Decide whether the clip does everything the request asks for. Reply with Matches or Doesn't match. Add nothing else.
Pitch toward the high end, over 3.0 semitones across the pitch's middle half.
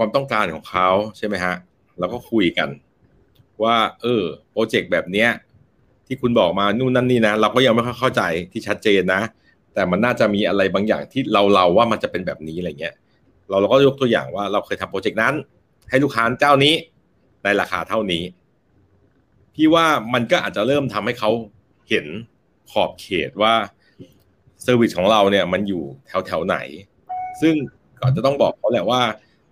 Doesn't match